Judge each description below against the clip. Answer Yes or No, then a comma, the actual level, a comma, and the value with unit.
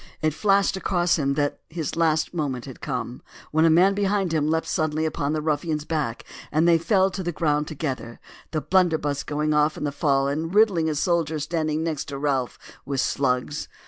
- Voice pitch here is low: No, medium, 155 Hz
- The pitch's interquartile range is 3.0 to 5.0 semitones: No, narrow, 2.6 semitones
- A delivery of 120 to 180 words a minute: No, average, 190 wpm